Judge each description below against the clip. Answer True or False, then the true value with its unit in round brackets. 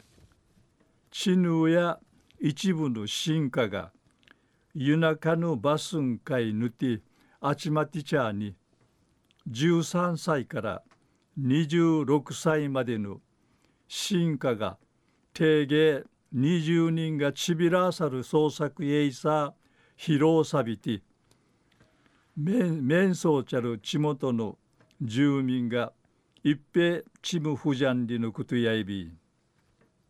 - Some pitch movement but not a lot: True (4.1 semitones)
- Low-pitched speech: False (150 Hz)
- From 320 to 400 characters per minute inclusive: False (170 characters per minute)